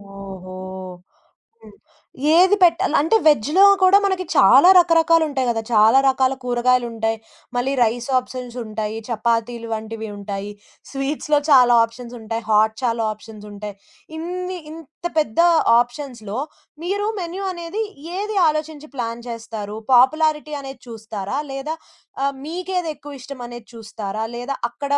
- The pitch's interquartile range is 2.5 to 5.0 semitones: No, wide, 5.6 semitones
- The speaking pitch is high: Yes, very high, 250 Hz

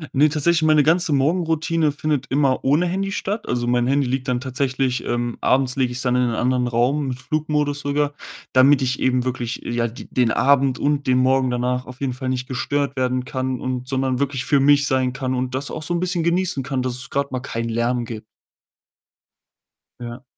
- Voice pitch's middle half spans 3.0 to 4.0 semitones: No, narrow, 2.4 semitones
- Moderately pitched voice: No, low, 130 Hz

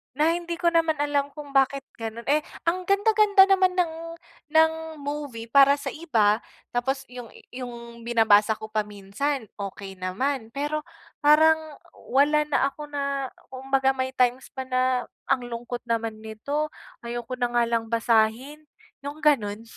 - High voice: Yes, very high, 265 Hz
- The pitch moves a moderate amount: Yes, average, 4.4 semitones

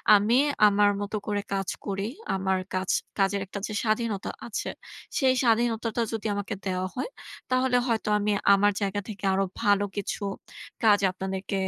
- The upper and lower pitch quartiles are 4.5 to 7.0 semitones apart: No, narrow, 2.4 semitones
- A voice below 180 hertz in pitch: No, high, 205 Hz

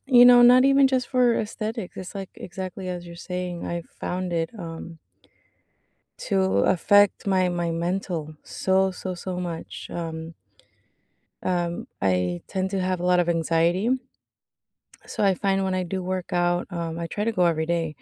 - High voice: No, medium, 180 Hz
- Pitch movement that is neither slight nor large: No, narrow, 2.2 semitones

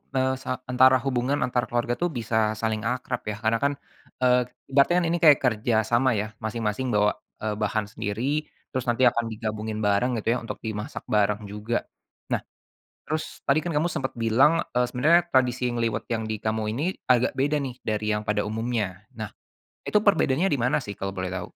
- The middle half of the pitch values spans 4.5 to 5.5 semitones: No, average, 3.4 semitones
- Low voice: Yes, low, 120 Hz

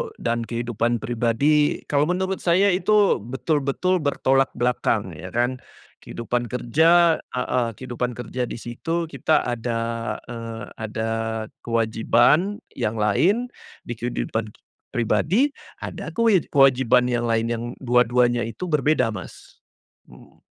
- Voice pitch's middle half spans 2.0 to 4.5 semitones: No, average, 5.2 semitones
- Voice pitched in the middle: No, low, 125 Hz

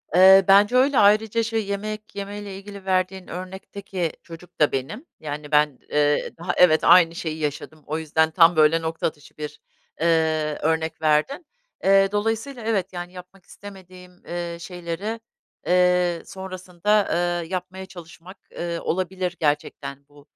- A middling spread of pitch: Yes, average, 3.4 semitones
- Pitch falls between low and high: Yes, medium, 180 Hz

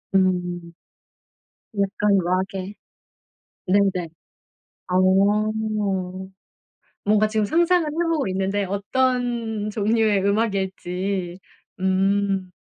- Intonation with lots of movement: No, narrow, 2.4 semitones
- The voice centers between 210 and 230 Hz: No, high, 200 Hz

